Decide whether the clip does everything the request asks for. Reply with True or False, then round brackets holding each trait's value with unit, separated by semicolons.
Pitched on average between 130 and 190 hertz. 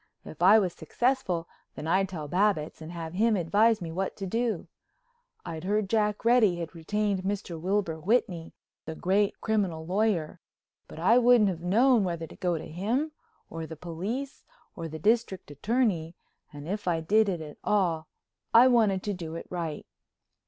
True (185 Hz)